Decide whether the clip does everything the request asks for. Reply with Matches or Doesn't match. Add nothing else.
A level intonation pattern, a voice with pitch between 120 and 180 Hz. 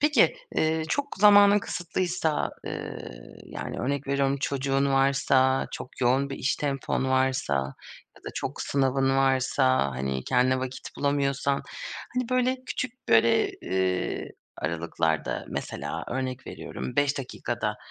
Matches